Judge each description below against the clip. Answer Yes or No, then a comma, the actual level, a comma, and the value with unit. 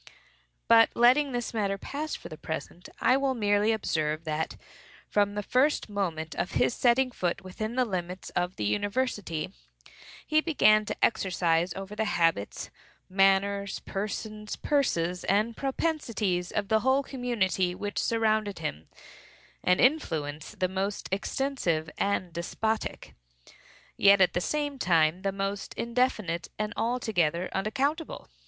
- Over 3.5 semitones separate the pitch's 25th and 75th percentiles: Yes, average, 5.1 semitones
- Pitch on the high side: Yes, high, 205 Hz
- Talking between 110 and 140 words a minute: Yes, slow, 135 wpm